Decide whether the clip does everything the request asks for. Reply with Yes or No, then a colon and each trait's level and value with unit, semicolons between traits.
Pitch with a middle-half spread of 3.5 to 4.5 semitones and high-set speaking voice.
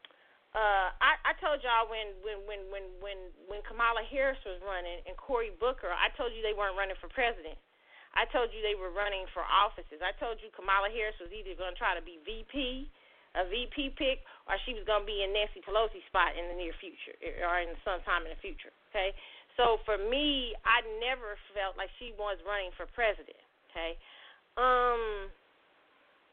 Yes: average, 3.9 semitones; high, 210 Hz